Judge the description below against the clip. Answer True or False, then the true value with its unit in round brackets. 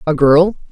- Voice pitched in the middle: True (160 Hz)